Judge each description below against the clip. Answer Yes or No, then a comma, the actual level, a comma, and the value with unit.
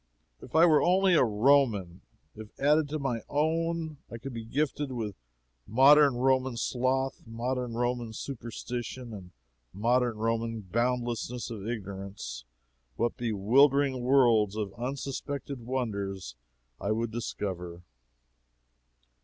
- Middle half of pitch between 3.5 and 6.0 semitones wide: Yes, average, 3.8 semitones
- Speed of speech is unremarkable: No, slow, 120 wpm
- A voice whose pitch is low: Yes, low, 120 Hz